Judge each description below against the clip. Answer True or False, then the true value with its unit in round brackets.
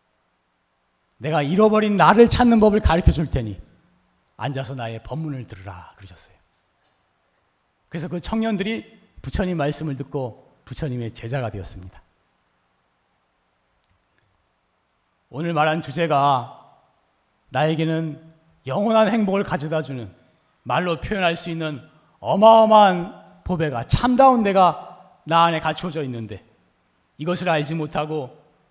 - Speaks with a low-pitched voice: False (155 Hz)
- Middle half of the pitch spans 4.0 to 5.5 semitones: False (7.4 semitones)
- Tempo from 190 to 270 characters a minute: True (255 characters per minute)